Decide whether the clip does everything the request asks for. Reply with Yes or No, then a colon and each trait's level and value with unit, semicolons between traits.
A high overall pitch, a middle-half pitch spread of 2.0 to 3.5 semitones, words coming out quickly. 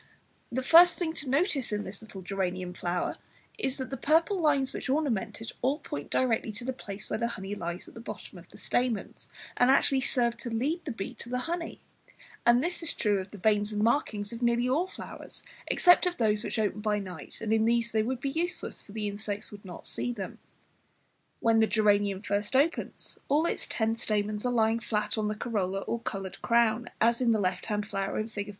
No: high, 225 Hz; average, 3.9 semitones; fast, 220 wpm